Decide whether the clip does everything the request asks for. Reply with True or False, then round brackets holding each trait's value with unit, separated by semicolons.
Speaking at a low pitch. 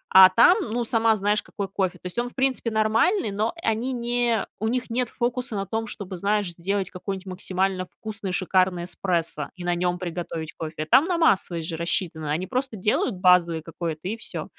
False (195 Hz)